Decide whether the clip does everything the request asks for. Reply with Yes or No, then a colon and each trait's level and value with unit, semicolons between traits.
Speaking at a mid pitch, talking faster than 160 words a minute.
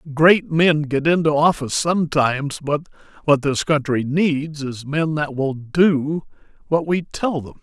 Yes: medium, 150 Hz; average, 175 wpm